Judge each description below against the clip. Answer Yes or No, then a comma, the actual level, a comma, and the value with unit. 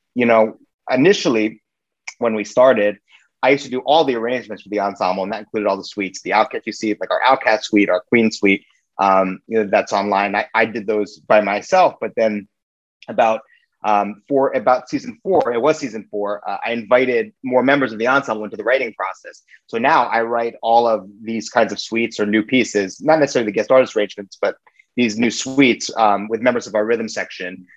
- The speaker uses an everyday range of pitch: Yes, average, 3.3 semitones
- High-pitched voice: No, low, 110 Hz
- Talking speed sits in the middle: No, fast, 210 wpm